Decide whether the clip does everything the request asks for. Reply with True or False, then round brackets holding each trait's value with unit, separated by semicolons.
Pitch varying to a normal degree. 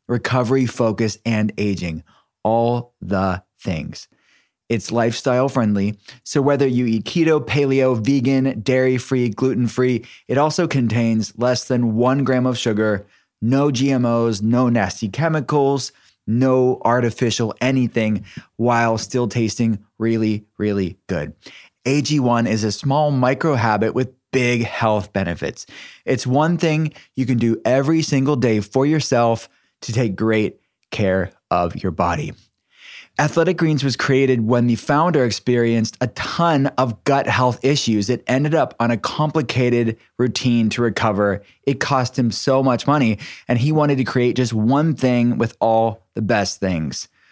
True (3.1 semitones)